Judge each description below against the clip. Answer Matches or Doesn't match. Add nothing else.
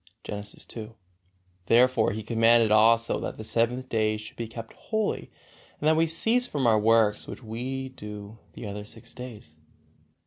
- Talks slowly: Doesn't match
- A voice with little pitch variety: Doesn't match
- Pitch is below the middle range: Matches